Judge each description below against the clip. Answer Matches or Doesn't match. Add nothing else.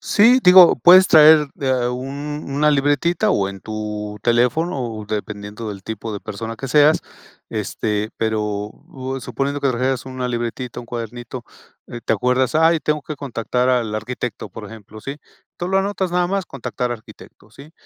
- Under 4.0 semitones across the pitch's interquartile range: Doesn't match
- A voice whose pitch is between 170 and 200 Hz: Doesn't match